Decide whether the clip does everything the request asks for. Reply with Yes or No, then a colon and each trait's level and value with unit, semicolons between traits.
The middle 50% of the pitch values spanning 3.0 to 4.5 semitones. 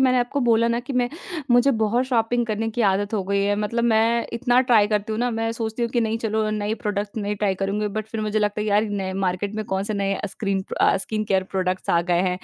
No: narrow, 2.6 semitones